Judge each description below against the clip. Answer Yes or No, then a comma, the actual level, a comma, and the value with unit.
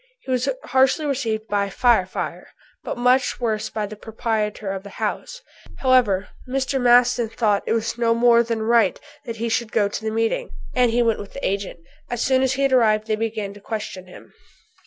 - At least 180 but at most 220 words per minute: Yes, average, 200 wpm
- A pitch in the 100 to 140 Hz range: No, high, 225 Hz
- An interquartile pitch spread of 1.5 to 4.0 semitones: Yes, average, 2.7 semitones